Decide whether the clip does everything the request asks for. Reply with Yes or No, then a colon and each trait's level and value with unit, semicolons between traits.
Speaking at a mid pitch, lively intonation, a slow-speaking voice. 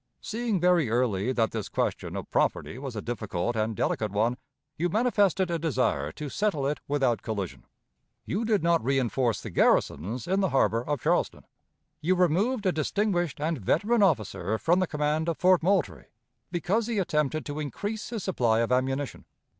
No: medium, 150 Hz; wide, 7.8 semitones; average, 170 wpm